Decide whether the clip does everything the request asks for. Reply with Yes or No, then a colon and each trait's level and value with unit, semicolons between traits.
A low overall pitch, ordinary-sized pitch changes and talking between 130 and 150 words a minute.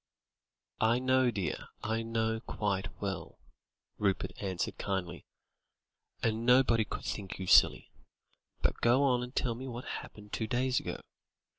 Yes: low, 115 Hz; average, 3.5 semitones; average, 140 wpm